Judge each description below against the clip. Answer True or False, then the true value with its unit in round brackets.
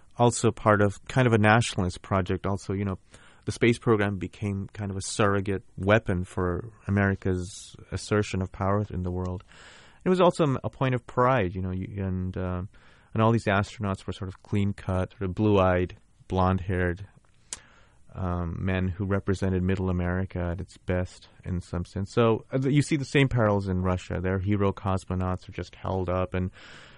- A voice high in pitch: False (95 Hz)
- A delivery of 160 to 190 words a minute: True (175 wpm)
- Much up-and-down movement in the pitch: False (2.8 semitones)